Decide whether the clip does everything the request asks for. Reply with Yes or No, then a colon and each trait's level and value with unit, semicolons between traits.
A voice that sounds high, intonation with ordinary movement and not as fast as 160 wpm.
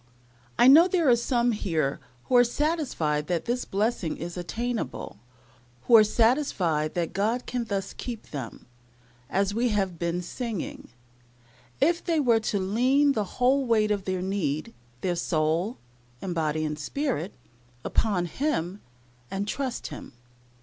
No: high, 210 Hz; wide, 6.2 semitones; average, 145 wpm